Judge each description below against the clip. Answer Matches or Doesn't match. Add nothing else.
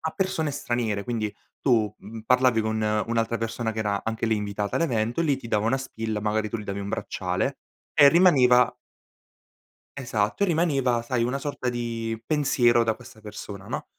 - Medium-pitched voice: Doesn't match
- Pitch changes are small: Doesn't match